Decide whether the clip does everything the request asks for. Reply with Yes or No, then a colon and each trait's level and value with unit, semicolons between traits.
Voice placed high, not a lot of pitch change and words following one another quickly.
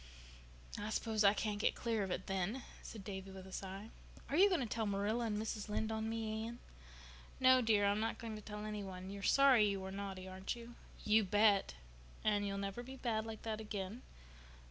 Yes: high, 215 Hz; narrow, 2.2 semitones; fast, 215 wpm